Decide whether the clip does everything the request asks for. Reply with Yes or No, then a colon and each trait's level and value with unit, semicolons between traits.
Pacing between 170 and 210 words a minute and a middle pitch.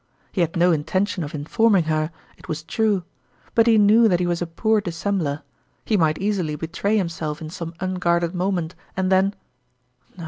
Yes: average, 185 wpm; medium, 175 Hz